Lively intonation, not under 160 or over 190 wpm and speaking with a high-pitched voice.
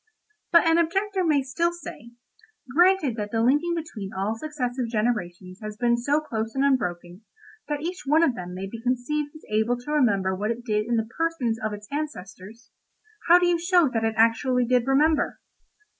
Yes: wide, 6.1 semitones; average, 185 wpm; high, 245 Hz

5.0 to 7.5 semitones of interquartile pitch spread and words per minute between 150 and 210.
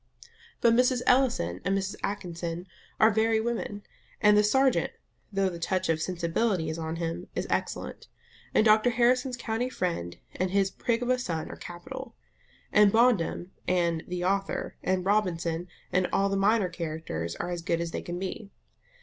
No: average, 4.6 semitones; average, 170 wpm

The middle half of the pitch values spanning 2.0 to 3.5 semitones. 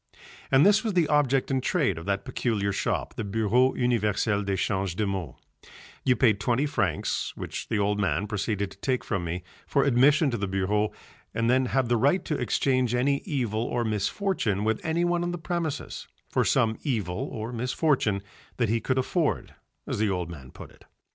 No: average, 5.3 semitones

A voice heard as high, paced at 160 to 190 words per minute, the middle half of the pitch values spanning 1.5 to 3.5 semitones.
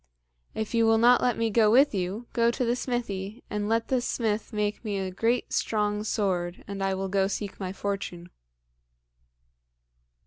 Yes: high, 210 Hz; average, 175 wpm; average, 3.0 semitones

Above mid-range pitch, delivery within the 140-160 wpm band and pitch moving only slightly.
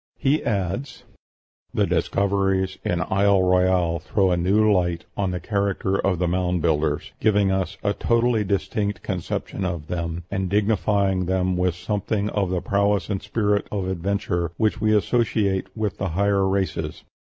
No: very low, 95 Hz; average, 155 wpm; narrow, 2.1 semitones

